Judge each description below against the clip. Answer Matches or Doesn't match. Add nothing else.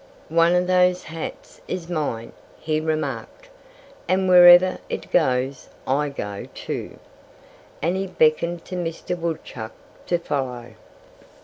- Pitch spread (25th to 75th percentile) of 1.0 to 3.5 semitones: Doesn't match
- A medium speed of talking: Doesn't match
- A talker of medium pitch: Matches